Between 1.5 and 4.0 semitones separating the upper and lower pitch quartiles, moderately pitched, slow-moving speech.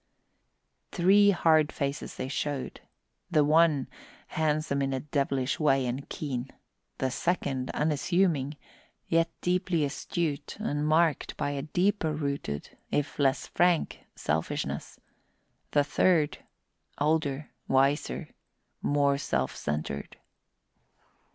Yes: average, 2.9 semitones; medium, 145 Hz; slow, 105 wpm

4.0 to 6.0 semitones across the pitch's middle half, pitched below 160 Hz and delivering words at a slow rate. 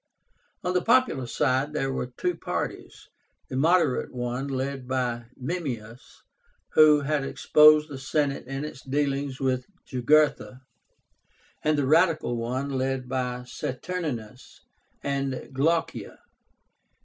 No: average, 2.9 semitones; low, 135 Hz; slow, 115 wpm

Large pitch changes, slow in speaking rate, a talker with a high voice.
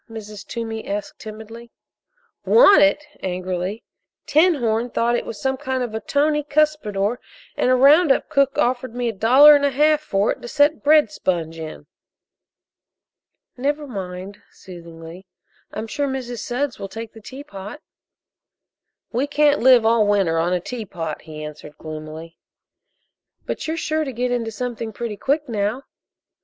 No: wide, 6.2 semitones; average, 155 wpm; high, 235 Hz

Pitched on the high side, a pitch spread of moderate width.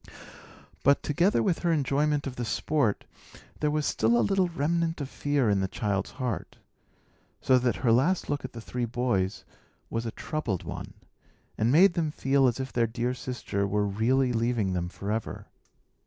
No: low, 125 Hz; average, 4.7 semitones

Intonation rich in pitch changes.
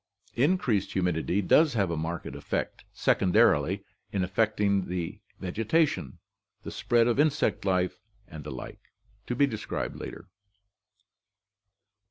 No: average, 4.8 semitones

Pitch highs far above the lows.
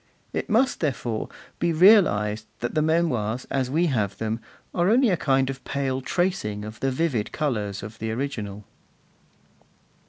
Yes: wide, 7.2 semitones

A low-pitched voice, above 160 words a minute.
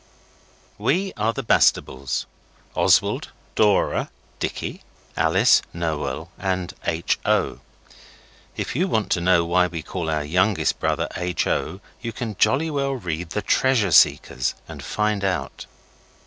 No: very low, 95 Hz; slow, 135 wpm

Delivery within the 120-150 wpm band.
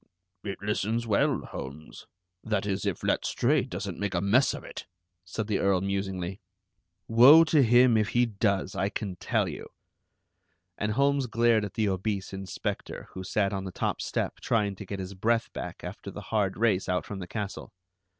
No: average, 180 wpm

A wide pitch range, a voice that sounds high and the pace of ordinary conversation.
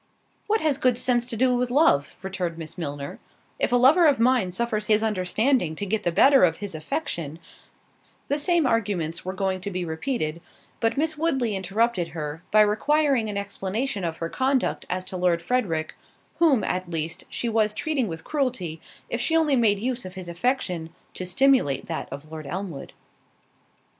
Yes: wide, 6.8 semitones; high, 210 Hz; average, 180 wpm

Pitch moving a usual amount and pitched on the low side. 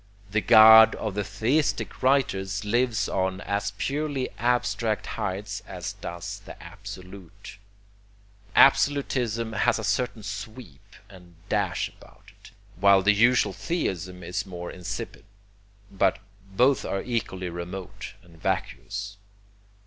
Yes: average, 4.0 semitones; low, 105 Hz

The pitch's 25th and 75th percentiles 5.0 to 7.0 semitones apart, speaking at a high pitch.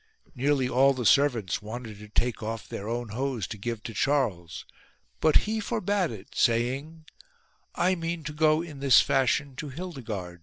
No: wide, 5.4 semitones; low, 130 Hz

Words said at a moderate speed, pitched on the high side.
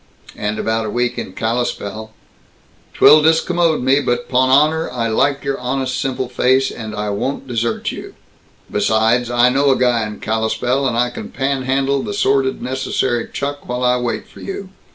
No: average, 175 wpm; low, 125 Hz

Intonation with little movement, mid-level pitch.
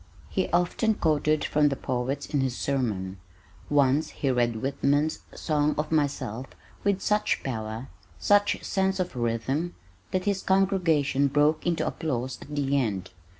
No: average, 4.6 semitones; medium, 145 Hz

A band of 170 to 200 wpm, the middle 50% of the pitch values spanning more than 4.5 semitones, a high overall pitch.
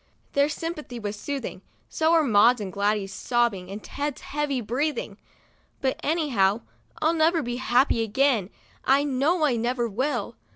No: average, 155 wpm; average, 5.3 semitones; very high, 255 Hz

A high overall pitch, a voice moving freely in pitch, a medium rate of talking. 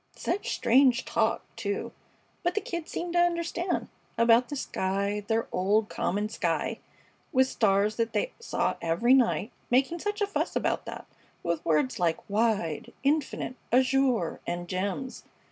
Yes: high, 230 Hz; wide, 5.8 semitones; average, 145 wpm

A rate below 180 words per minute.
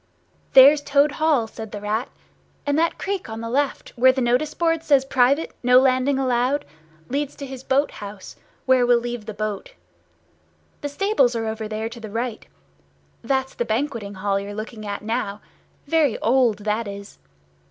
Yes: average, 170 wpm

